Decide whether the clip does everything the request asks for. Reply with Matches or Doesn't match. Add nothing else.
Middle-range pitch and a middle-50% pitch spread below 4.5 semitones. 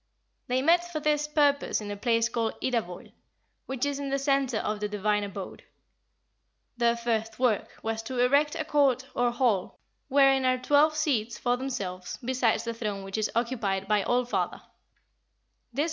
Doesn't match